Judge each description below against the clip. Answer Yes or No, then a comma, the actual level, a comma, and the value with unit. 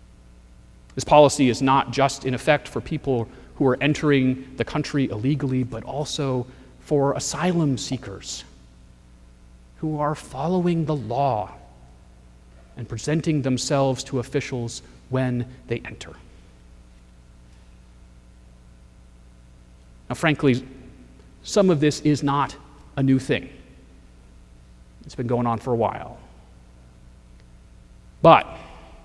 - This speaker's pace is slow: Yes, slow, 105 wpm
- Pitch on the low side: Yes, low, 115 Hz